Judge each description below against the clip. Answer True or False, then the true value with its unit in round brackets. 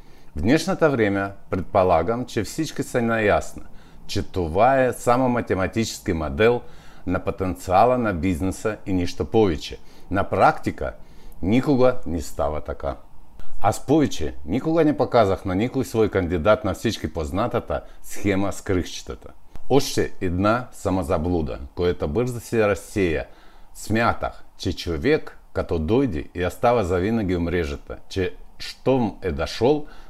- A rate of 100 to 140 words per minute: True (115 wpm)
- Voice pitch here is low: True (100 Hz)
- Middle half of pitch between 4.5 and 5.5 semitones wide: True (4.9 semitones)